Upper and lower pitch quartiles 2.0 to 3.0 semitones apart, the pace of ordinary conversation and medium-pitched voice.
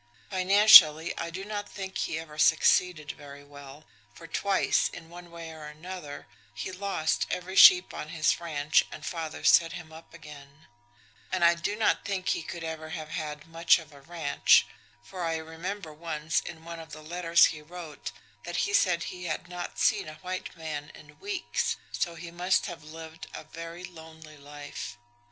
Yes: narrow, 2.4 semitones; average, 180 wpm; medium, 165 Hz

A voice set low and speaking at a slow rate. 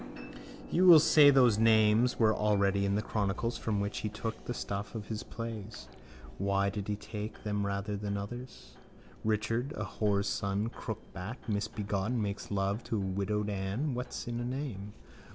No: low, 105 Hz; average, 170 wpm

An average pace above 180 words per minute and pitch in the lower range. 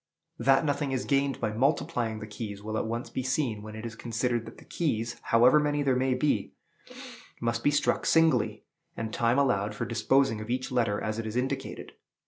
Yes: average, 200 wpm; low, 120 Hz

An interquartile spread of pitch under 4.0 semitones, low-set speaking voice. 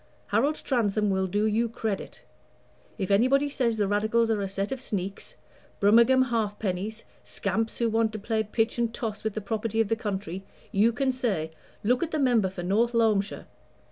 No: average, 2.7 semitones; high, 220 Hz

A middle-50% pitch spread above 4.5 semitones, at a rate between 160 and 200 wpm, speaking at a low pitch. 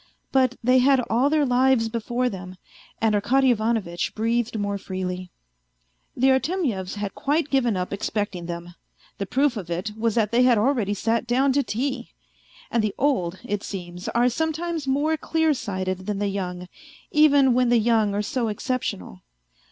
No: average, 4.9 semitones; average, 165 wpm; high, 230 Hz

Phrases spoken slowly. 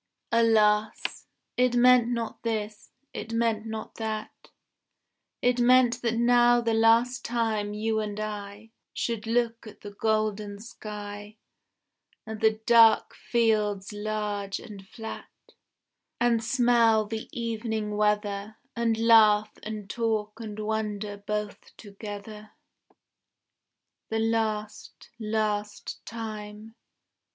Yes: slow, 110 wpm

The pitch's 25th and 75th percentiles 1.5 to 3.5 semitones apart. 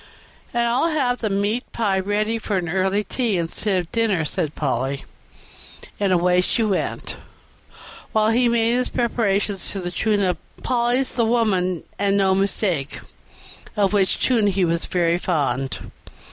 No: average, 4.1 semitones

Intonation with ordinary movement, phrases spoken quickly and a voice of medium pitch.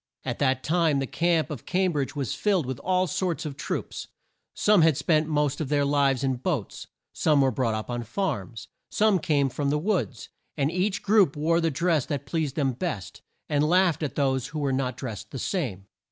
Yes: average, 4.2 semitones; fast, 210 wpm; medium, 150 Hz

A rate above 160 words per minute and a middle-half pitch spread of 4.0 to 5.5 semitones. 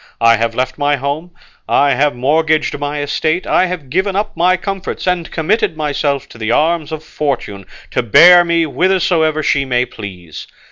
Yes: average, 175 wpm; average, 4.5 semitones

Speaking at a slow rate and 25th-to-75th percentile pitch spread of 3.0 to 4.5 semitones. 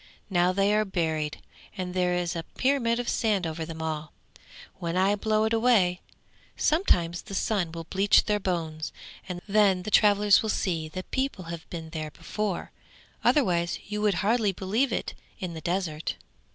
No: average, 165 wpm; average, 3.9 semitones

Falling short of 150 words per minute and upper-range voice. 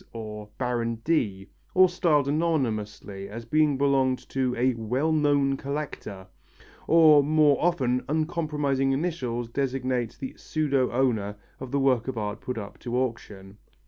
No: average, 140 wpm; low, 130 Hz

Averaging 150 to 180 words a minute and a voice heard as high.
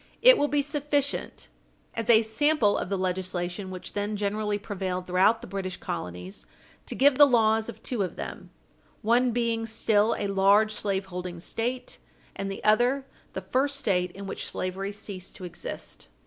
Yes: average, 165 wpm; high, 205 Hz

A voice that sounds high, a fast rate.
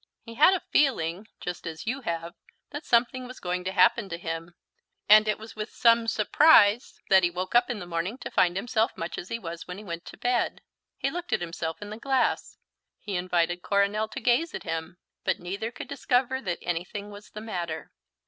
Yes: high, 205 Hz; fast, 210 wpm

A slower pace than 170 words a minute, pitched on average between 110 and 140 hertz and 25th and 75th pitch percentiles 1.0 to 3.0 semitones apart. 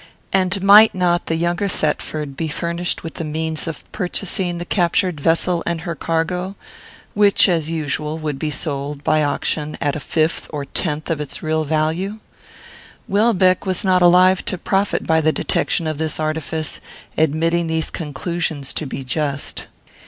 No: average, 160 wpm; medium, 165 Hz; narrow, 2.6 semitones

